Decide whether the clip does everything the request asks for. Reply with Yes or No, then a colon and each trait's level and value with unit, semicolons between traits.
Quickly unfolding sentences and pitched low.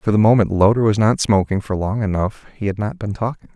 Yes: fast, 255 wpm; low, 105 Hz